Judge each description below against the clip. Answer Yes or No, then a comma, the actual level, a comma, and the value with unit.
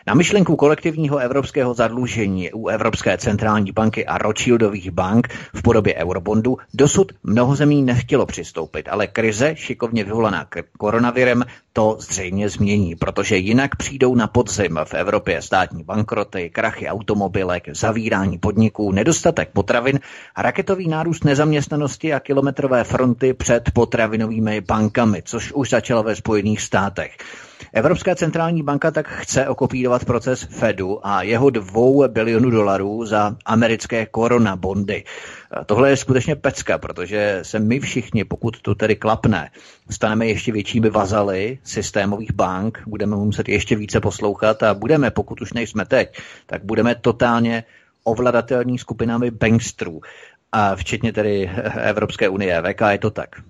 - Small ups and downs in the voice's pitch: No, average, 3.4 semitones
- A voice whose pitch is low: Yes, low, 115 Hz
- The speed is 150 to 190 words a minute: No, average, 135 wpm